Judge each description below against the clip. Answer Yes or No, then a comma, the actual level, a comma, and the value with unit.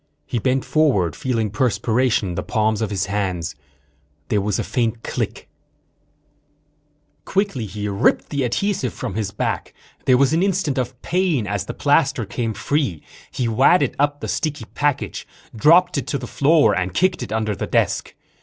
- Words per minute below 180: Yes, average, 170 wpm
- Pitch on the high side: No, low, 125 Hz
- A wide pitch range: Yes, wide, 5.7 semitones